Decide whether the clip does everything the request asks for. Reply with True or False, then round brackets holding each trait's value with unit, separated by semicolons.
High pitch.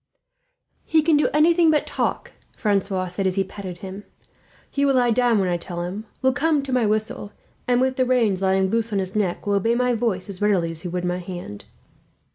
True (205 Hz)